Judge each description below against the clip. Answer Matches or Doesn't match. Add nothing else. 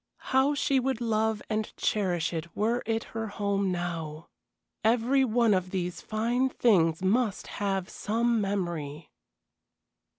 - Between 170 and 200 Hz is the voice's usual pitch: Doesn't match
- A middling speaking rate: Doesn't match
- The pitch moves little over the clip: Doesn't match